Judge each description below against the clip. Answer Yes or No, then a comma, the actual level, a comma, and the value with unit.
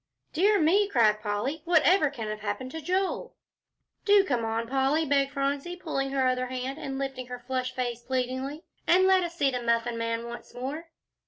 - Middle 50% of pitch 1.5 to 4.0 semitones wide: No, average, 4.6 semitones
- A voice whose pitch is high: Yes, very high, 270 Hz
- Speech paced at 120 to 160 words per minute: No, average, 190 wpm